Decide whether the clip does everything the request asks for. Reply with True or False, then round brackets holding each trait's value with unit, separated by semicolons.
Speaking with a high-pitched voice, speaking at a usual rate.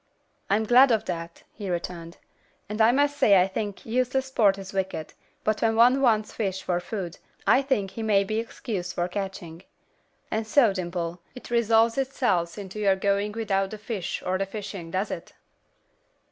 True (205 Hz; 175 wpm)